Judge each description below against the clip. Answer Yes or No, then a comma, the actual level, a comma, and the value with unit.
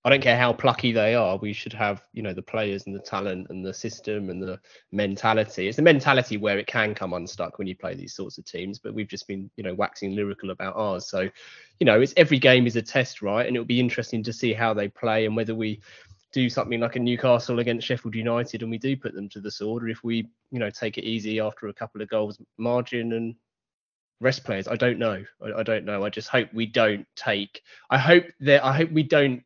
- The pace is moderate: No, fast, 255 wpm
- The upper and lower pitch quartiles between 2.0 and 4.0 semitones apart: Yes, average, 2.9 semitones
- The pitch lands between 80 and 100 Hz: No, low, 110 Hz